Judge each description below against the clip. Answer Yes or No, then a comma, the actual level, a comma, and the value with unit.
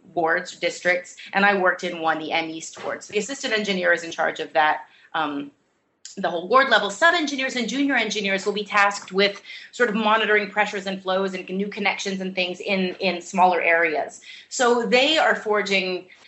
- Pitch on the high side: Yes, high, 195 Hz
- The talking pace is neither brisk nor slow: Yes, average, 195 wpm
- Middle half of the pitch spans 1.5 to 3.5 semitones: Yes, average, 3.2 semitones